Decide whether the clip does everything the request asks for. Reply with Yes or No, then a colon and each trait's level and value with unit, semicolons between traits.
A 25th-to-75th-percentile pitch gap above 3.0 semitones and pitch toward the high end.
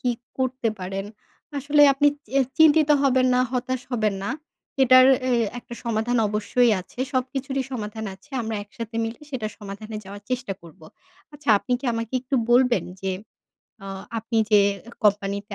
Yes: average, 3.7 semitones; high, 235 Hz